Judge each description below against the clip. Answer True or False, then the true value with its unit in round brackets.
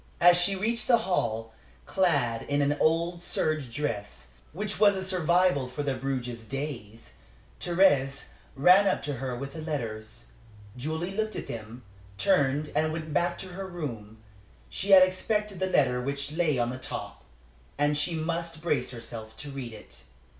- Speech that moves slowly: False (160 wpm)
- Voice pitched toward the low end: False (145 Hz)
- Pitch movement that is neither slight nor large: False (6.1 semitones)